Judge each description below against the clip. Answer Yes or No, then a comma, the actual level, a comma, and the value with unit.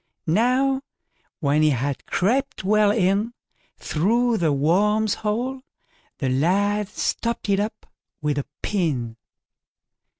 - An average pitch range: No, wide, 6.5 semitones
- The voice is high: Yes, high, 205 Hz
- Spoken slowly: Yes, slow, 110 wpm